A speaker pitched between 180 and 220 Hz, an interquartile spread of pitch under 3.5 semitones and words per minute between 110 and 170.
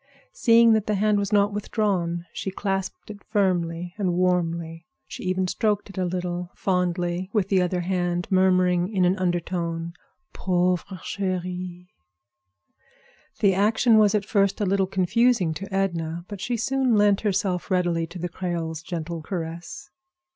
Yes: medium, 185 Hz; narrow, 2.5 semitones; average, 150 wpm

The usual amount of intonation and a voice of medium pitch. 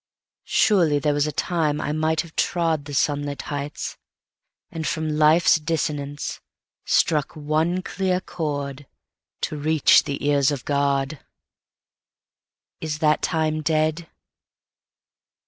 No: narrow, 1.8 semitones; medium, 155 Hz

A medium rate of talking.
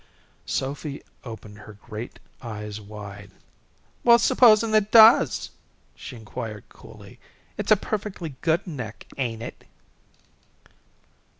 No: slow, 105 wpm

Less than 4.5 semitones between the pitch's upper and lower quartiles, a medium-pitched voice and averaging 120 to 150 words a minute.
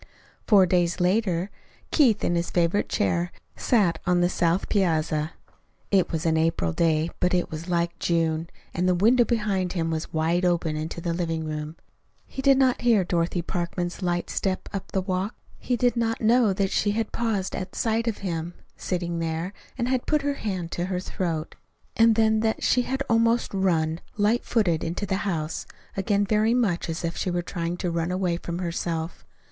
No: average, 4.0 semitones; medium, 180 Hz; average, 190 wpm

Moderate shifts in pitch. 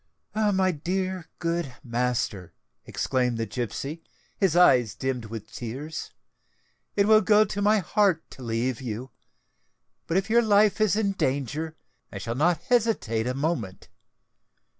No: wide, 8.2 semitones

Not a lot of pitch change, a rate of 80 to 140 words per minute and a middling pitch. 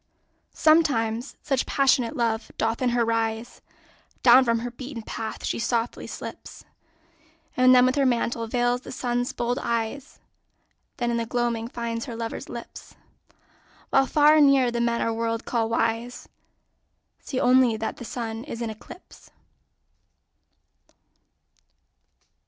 No: narrow, 1.9 semitones; slow, 135 wpm; high, 235 Hz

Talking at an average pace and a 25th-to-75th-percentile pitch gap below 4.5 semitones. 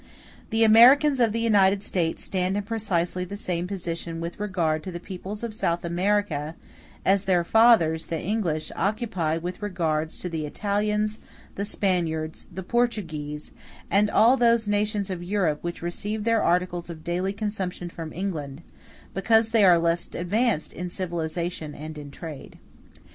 Yes: average, 155 wpm; average, 3.9 semitones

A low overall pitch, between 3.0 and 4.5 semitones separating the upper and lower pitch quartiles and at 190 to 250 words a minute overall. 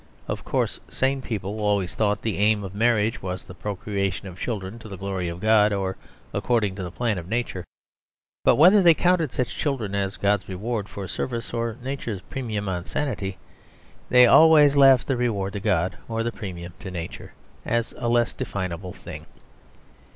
No: low, 105 Hz; average, 3.9 semitones; average, 180 wpm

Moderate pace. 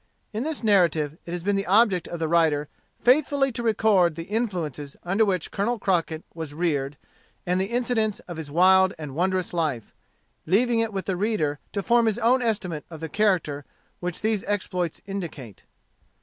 Yes: average, 180 wpm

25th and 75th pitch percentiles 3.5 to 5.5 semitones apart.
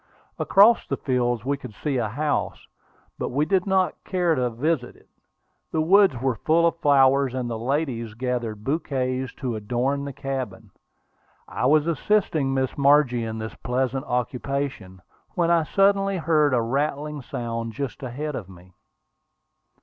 Yes: average, 4.1 semitones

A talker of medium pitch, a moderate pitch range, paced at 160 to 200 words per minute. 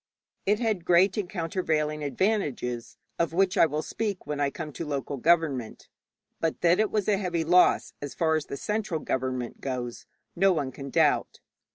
Yes: medium, 160 Hz; average, 5.0 semitones; average, 180 wpm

